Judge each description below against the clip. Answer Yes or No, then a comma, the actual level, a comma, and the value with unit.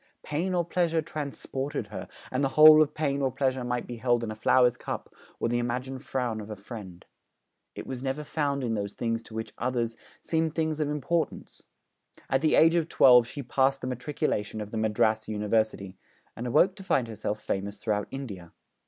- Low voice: Yes, low, 125 Hz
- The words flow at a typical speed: Yes, average, 195 wpm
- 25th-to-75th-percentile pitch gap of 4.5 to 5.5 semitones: Yes, average, 5.0 semitones